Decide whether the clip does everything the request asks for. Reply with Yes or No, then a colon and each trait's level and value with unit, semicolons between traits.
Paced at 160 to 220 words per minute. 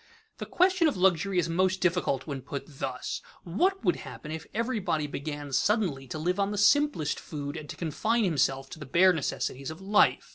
Yes: average, 195 wpm